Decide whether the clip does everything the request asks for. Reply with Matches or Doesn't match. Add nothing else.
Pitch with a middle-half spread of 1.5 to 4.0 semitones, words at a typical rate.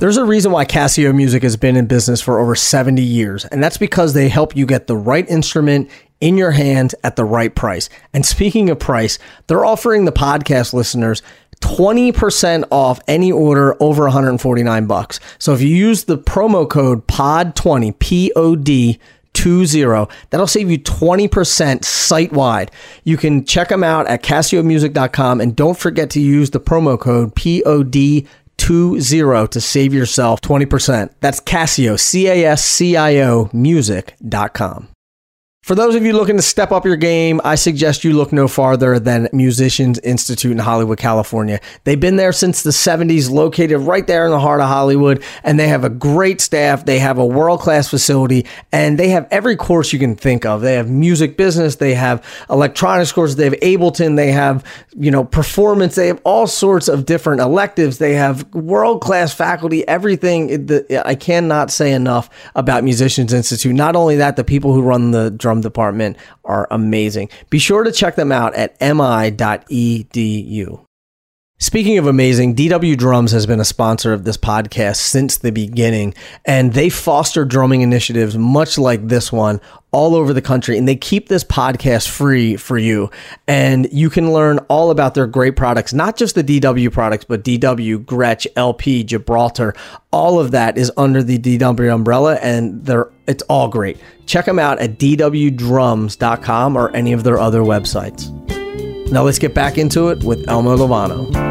Doesn't match